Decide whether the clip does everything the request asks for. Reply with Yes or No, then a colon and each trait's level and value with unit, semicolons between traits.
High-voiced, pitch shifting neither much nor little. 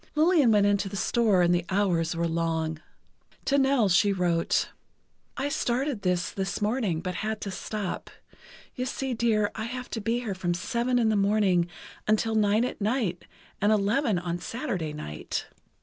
Yes: high, 205 Hz; average, 4.8 semitones